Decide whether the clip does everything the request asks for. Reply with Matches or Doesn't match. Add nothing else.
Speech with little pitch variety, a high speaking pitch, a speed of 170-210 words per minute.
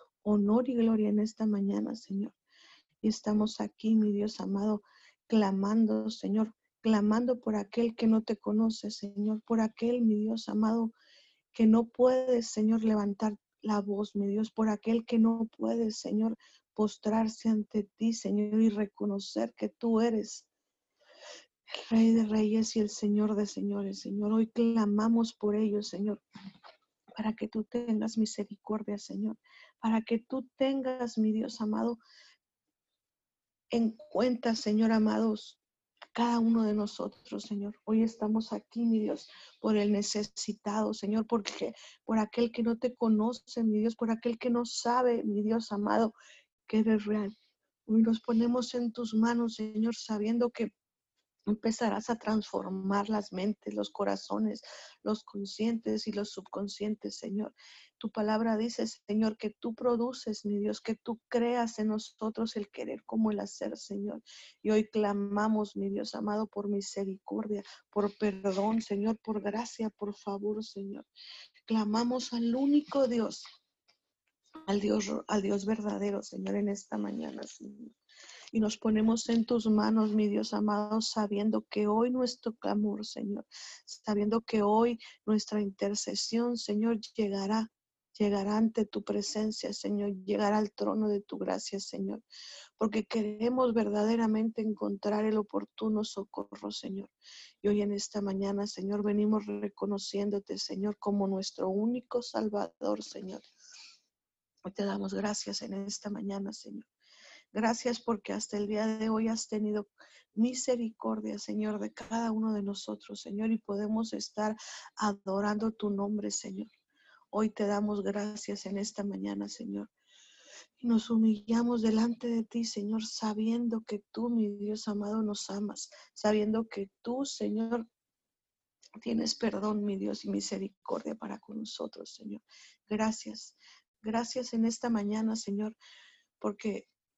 Doesn't match